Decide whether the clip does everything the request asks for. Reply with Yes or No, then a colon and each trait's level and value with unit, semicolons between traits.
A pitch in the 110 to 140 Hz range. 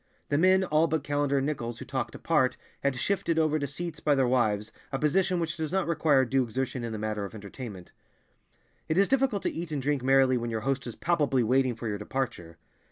Yes: low, 135 Hz